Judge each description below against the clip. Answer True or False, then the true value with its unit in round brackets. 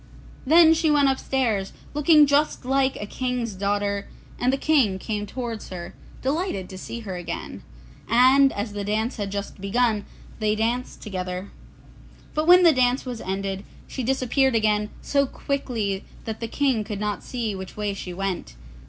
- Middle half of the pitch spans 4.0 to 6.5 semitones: True (4.8 semitones)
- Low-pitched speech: False (225 Hz)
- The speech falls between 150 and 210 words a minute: True (165 wpm)